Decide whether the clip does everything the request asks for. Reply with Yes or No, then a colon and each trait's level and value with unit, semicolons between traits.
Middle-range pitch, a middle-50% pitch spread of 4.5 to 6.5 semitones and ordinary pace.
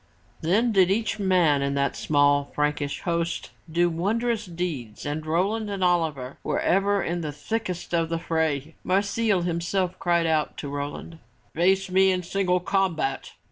No: medium, 175 Hz; average, 3.8 semitones; average, 155 wpm